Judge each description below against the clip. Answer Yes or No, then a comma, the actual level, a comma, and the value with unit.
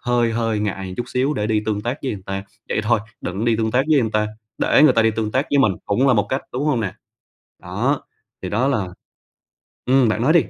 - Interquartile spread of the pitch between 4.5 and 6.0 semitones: No, average, 3.6 semitones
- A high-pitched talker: No, low, 115 Hz